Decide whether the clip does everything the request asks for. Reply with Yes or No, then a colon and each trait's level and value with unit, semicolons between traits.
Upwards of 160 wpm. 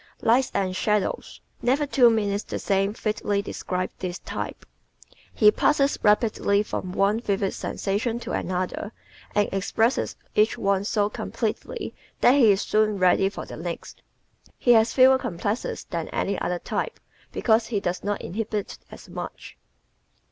No: average, 150 wpm